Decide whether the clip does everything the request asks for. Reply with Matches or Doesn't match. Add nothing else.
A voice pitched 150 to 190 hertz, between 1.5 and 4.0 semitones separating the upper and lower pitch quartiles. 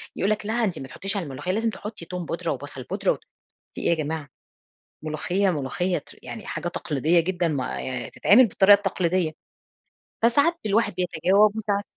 Doesn't match